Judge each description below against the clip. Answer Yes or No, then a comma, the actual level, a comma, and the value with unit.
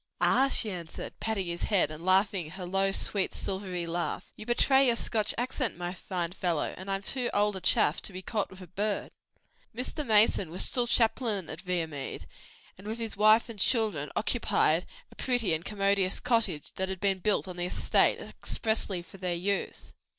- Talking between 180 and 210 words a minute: Yes, average, 185 wpm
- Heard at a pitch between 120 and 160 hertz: No, high, 195 Hz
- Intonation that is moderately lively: Yes, average, 3.5 semitones